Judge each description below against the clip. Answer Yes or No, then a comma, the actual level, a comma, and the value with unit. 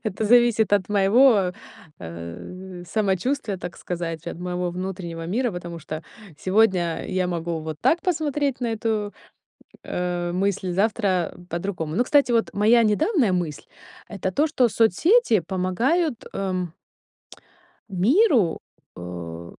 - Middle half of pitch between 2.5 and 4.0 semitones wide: No, average, 4.8 semitones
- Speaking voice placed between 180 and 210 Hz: Yes, high, 190 Hz